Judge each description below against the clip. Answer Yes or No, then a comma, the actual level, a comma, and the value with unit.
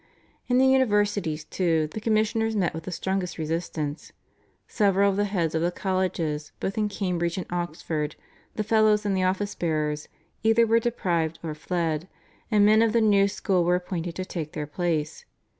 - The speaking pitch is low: No, medium, 185 Hz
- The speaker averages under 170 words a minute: No, average, 175 wpm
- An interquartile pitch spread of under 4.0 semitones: No, average, 4.3 semitones